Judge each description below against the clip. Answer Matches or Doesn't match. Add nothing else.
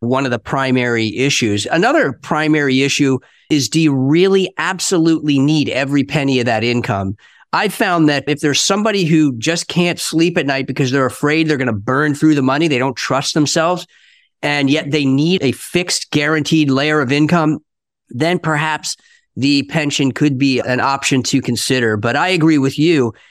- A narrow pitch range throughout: Doesn't match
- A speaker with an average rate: Matches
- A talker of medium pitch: Matches